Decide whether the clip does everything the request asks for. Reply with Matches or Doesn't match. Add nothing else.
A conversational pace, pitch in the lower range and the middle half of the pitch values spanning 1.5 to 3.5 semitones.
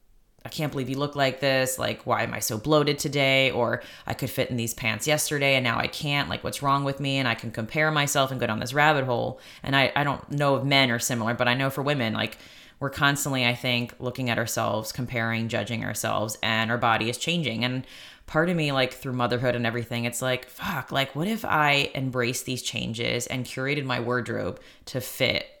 Doesn't match